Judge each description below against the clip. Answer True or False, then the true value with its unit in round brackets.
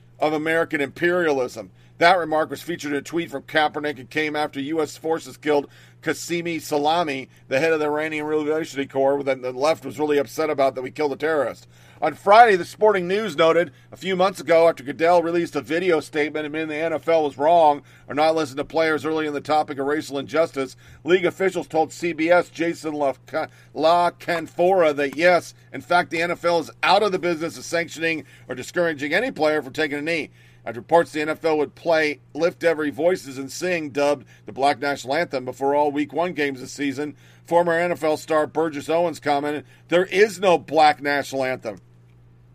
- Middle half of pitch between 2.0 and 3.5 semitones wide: True (3.1 semitones)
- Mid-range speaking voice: True (150 Hz)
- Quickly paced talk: False (190 wpm)